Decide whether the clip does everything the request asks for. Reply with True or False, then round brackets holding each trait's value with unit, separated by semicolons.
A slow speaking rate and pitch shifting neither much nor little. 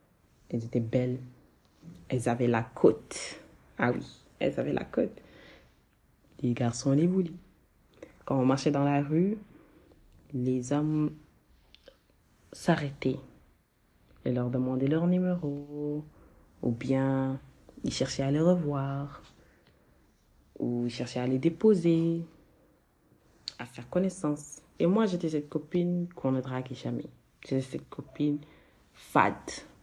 True (120 wpm; 3.9 semitones)